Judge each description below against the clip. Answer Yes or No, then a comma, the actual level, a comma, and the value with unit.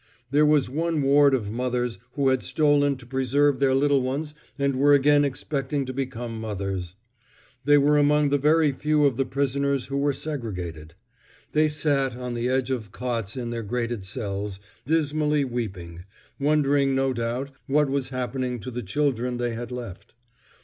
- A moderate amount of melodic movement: Yes, average, 3.1 semitones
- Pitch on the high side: No, low, 135 Hz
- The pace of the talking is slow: No, average, 170 wpm